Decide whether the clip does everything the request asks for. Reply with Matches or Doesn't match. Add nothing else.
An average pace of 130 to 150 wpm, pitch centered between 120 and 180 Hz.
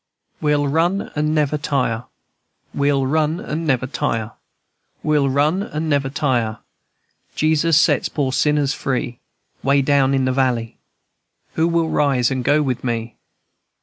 Matches